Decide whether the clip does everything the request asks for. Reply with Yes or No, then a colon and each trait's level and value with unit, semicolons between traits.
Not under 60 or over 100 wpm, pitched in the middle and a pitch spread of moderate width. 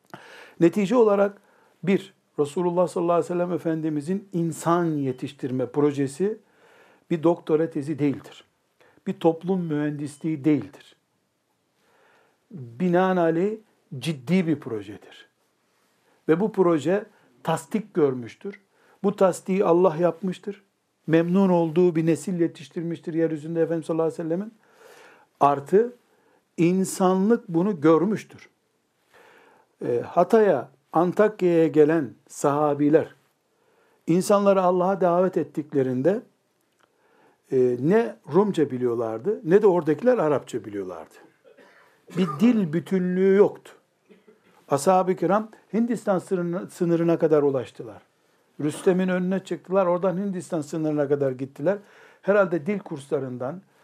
Yes: slow, 95 wpm; medium, 175 Hz; average, 4.0 semitones